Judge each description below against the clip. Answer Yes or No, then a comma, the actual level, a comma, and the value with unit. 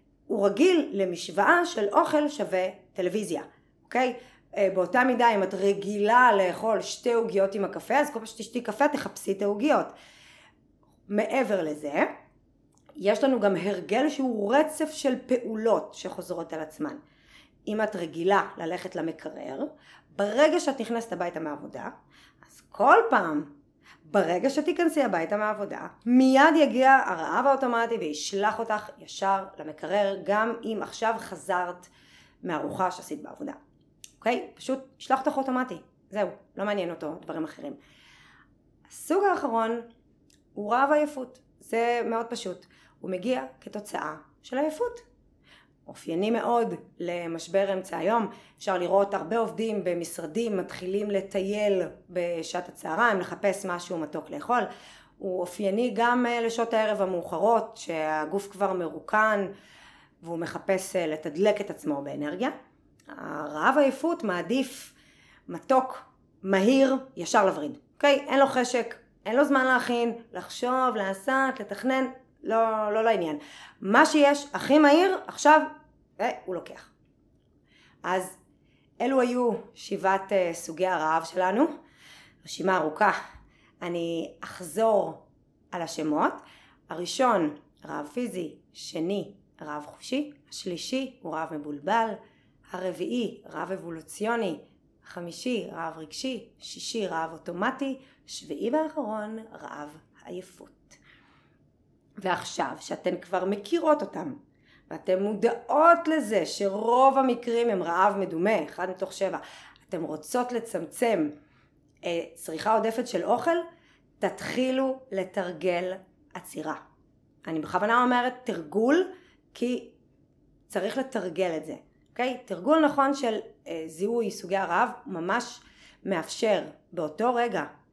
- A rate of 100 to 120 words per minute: Yes, average, 115 wpm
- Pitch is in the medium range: No, high, 210 Hz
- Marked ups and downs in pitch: Yes, wide, 5.7 semitones